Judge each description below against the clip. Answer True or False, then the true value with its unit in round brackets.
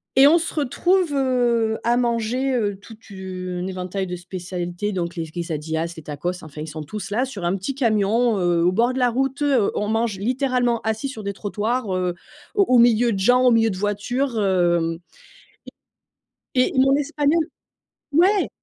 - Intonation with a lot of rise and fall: True (5.7 semitones)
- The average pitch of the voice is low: False (220 Hz)